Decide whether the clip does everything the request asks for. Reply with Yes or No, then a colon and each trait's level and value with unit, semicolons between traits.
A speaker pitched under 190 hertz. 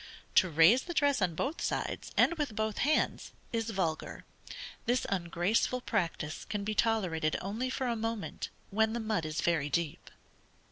No: high, 215 Hz